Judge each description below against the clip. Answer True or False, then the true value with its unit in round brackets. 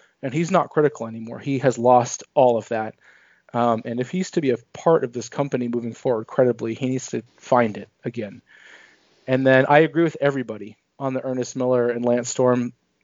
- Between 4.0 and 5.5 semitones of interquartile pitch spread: False (2.7 semitones)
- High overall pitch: False (125 Hz)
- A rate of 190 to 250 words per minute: True (200 wpm)